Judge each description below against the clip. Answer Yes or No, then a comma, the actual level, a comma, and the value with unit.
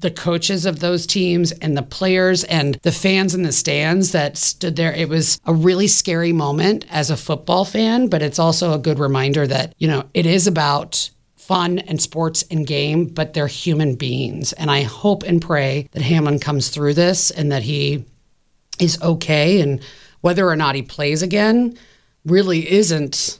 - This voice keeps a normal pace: Yes, average, 185 wpm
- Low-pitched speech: No, medium, 160 Hz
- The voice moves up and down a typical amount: Yes, average, 3.6 semitones